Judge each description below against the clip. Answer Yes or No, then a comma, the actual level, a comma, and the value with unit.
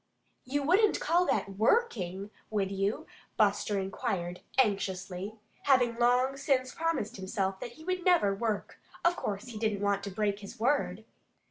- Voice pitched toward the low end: No, high, 215 Hz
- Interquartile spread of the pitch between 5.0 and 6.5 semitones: Yes, average, 5.3 semitones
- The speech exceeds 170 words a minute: No, average, 150 wpm